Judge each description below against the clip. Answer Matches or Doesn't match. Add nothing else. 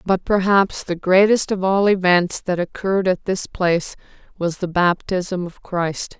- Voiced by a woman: Matches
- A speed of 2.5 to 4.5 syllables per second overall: Matches